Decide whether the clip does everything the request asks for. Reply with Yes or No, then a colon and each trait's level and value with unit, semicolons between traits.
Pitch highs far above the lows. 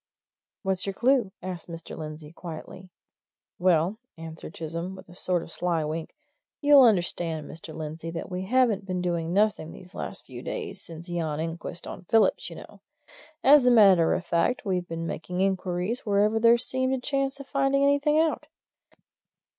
Yes: wide, 6.2 semitones